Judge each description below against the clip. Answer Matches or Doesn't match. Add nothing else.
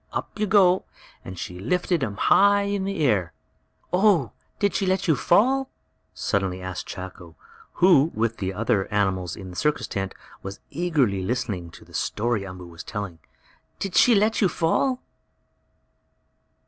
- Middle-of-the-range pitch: Doesn't match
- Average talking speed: Matches